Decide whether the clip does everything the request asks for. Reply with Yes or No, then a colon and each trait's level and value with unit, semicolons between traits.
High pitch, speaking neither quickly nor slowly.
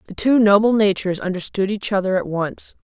Yes: high, 200 Hz; average, 190 wpm